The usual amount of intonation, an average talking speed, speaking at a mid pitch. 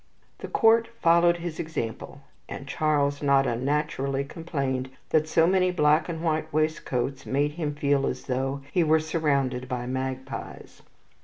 Yes: average, 3.1 semitones; average, 145 wpm; medium, 145 Hz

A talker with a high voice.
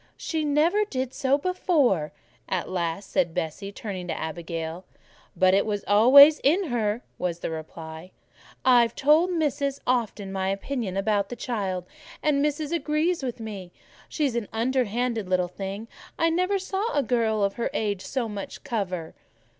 Yes: high, 225 Hz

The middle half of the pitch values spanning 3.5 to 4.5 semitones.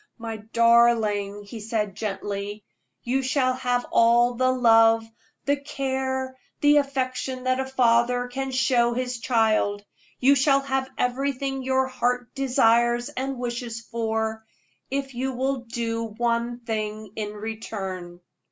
No: average, 2.7 semitones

